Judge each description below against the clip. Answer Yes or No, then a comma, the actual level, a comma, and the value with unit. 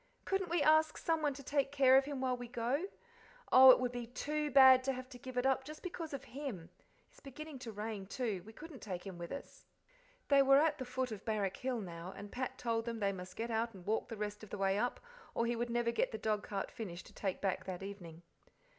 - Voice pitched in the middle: No, high, 240 Hz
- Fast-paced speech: Yes, fast, 245 wpm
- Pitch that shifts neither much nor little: Yes, average, 4.8 semitones